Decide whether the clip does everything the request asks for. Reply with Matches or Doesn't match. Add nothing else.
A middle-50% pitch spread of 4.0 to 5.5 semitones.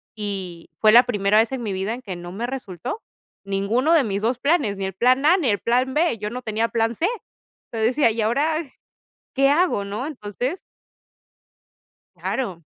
Matches